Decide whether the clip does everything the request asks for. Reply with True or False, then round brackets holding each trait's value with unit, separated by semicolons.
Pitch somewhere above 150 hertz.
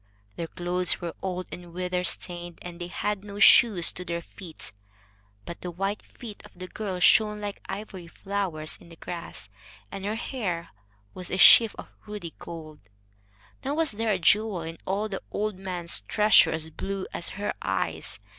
True (185 Hz)